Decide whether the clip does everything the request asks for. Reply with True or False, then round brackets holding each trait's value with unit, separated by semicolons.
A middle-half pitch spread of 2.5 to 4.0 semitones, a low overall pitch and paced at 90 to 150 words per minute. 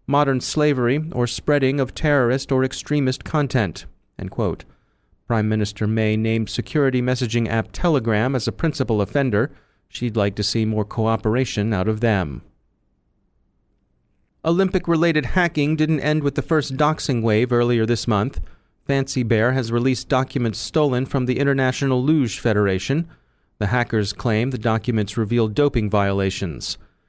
False (4.4 semitones; 120 Hz; 140 wpm)